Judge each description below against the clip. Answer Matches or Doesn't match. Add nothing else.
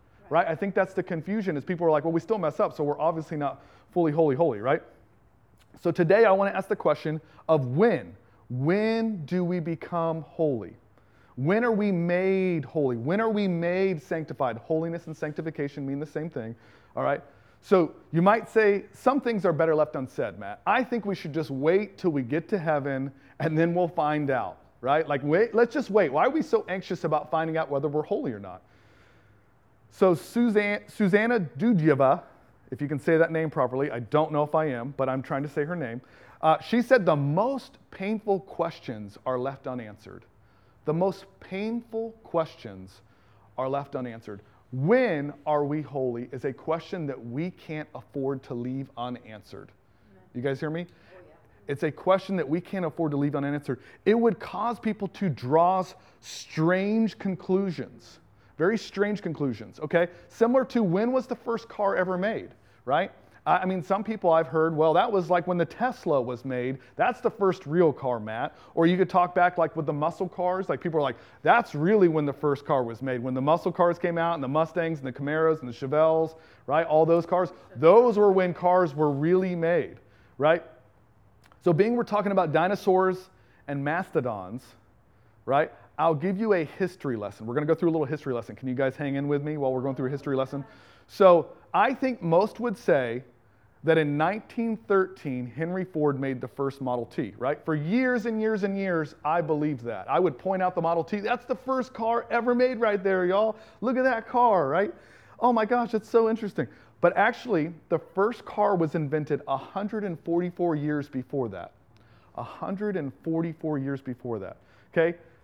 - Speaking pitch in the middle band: Matches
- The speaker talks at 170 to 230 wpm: Matches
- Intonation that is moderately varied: Doesn't match